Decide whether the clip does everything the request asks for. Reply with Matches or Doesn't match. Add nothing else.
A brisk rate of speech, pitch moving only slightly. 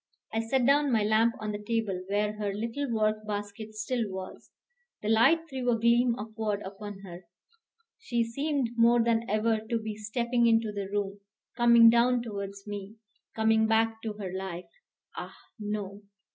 Doesn't match